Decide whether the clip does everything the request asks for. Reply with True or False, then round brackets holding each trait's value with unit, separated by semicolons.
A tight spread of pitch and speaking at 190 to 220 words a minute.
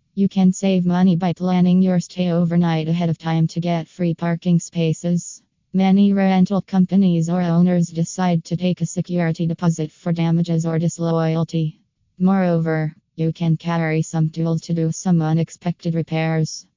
False (1.7 semitones; 155 wpm)